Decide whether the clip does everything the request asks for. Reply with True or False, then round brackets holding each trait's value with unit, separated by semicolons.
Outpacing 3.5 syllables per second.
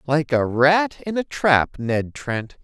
False (3.3 syllables/s)